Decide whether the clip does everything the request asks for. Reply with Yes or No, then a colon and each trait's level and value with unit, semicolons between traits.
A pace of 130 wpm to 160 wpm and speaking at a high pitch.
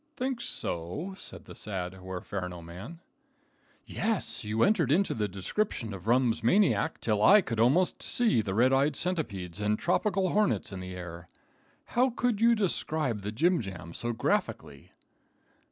No: average, 150 wpm; low, 120 Hz